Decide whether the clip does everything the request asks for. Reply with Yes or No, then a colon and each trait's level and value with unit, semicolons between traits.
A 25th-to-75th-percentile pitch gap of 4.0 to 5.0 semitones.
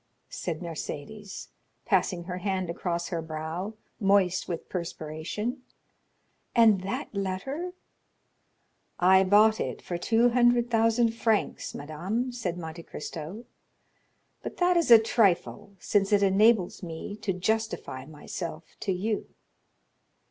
Yes: average, 4.6 semitones